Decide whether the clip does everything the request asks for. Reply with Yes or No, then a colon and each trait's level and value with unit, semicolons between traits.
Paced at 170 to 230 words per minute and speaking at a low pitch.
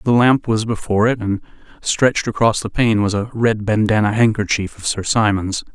Yes: average, 190 wpm; low, 110 Hz